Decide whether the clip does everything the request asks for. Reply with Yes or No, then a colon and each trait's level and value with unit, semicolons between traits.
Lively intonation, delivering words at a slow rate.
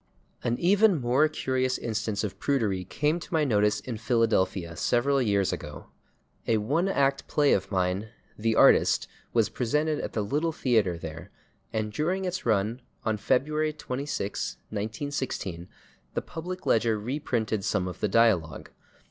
No: wide, 5.8 semitones; average, 150 wpm